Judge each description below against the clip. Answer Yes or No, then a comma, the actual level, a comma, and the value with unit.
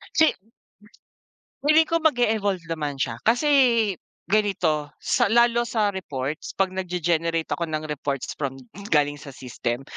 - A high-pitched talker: No, medium, 170 Hz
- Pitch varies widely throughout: Yes, wide, 6.8 semitones